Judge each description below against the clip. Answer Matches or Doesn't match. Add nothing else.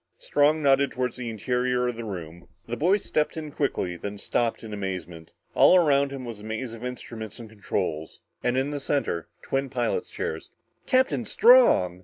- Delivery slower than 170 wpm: Doesn't match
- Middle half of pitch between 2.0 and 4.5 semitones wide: Doesn't match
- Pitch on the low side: Matches